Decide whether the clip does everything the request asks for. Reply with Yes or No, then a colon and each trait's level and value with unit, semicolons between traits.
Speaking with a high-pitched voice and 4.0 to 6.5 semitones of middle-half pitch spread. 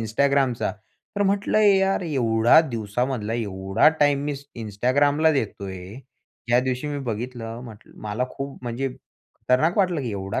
No: low, 125 Hz; average, 4.6 semitones